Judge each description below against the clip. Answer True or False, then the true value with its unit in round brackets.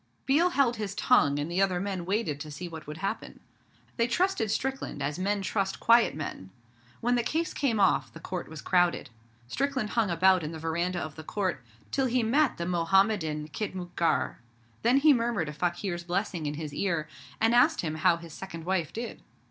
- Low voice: False (185 Hz)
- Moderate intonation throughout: False (6.2 semitones)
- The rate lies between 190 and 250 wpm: True (195 wpm)